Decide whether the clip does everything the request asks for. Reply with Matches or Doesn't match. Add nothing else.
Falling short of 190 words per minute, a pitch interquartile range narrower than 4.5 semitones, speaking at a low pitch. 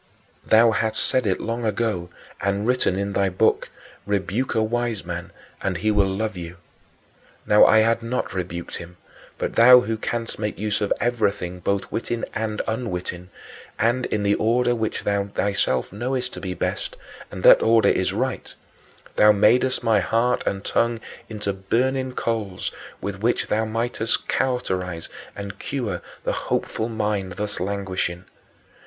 Matches